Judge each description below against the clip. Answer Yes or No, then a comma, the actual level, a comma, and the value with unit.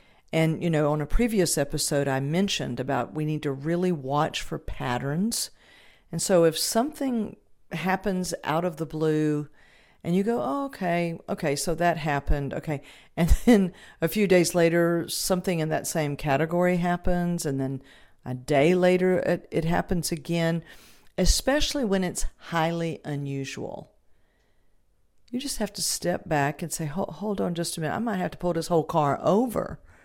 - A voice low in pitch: No, medium, 170 Hz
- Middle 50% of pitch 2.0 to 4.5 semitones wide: Yes, average, 3.3 semitones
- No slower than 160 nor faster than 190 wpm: Yes, average, 170 wpm